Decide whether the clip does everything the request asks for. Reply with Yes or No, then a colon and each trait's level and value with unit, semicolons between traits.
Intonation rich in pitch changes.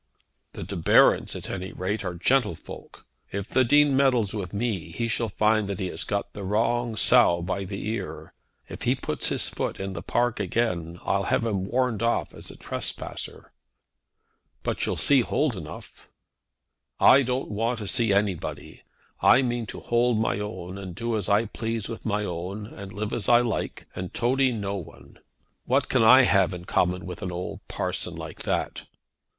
No: average, 3.7 semitones